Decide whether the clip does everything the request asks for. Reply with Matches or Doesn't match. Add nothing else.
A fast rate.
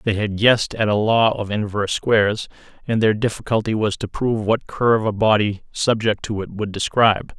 Doesn't match